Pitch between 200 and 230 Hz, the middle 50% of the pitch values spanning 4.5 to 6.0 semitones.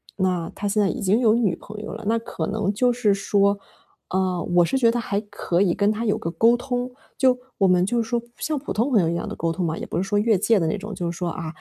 No: high, 205 Hz; average, 4.0 semitones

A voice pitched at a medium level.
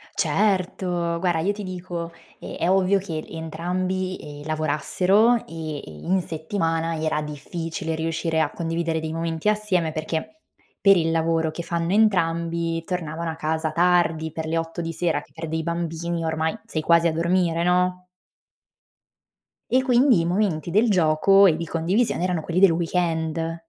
Yes: medium, 170 Hz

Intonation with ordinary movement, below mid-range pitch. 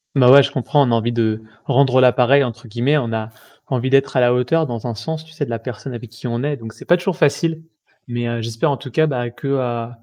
Yes: average, 3.2 semitones; low, 125 Hz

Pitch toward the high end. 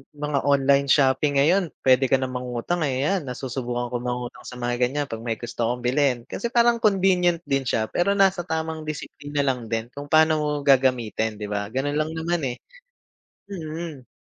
No: medium, 140 Hz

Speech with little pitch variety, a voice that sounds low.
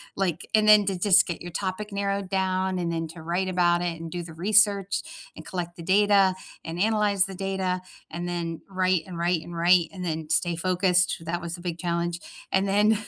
No: narrow, 2.1 semitones; medium, 180 Hz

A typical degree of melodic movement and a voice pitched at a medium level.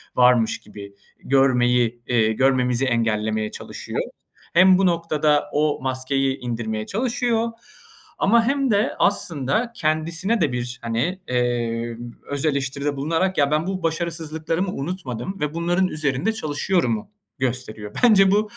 No: wide, 6.7 semitones; medium, 145 Hz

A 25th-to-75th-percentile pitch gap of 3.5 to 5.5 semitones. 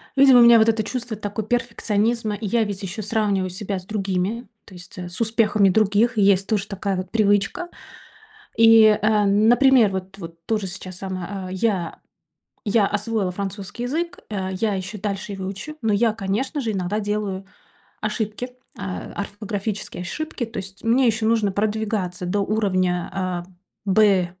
No: narrow, 2.6 semitones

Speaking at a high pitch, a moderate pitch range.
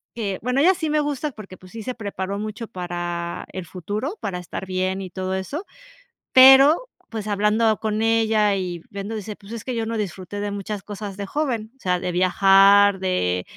Yes: high, 205 Hz; average, 3.3 semitones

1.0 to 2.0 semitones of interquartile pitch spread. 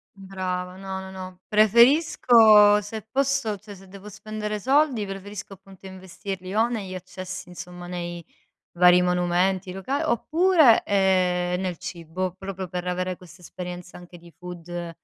No: average, 2.7 semitones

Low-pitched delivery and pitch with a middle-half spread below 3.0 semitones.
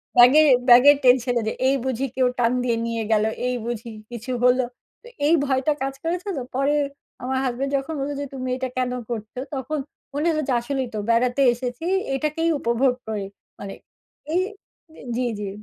No: very high, 255 Hz; narrow, 2.4 semitones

